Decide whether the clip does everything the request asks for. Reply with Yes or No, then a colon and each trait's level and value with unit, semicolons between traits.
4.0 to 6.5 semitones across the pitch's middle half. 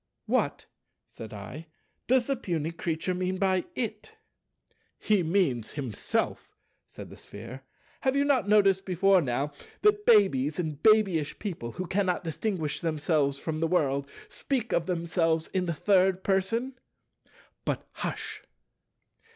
Yes: average, 4.6 semitones